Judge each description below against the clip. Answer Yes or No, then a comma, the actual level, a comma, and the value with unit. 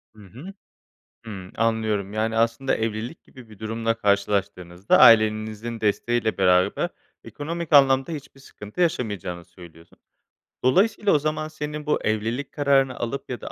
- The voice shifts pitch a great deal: No, average, 4.9 semitones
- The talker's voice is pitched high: No, low, 115 Hz